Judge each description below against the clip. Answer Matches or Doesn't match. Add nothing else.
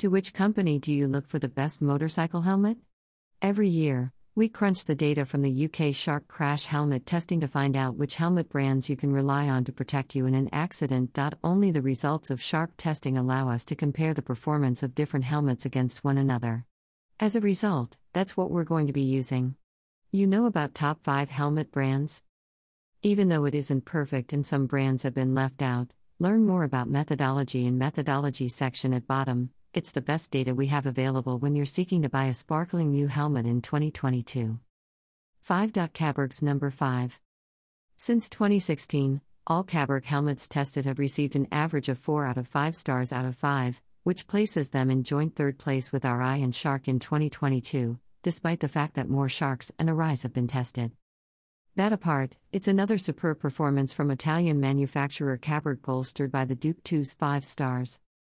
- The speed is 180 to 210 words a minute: Matches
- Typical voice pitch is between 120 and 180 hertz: Matches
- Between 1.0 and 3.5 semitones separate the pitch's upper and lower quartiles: Matches